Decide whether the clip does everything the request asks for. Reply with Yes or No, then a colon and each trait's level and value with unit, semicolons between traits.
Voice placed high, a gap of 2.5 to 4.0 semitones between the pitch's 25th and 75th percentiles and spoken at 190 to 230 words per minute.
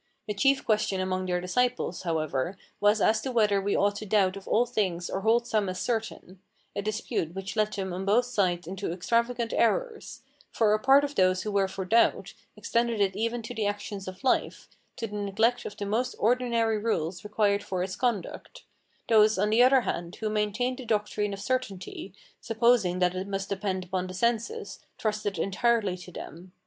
Yes: high, 210 Hz; average, 3.6 semitones; average, 195 wpm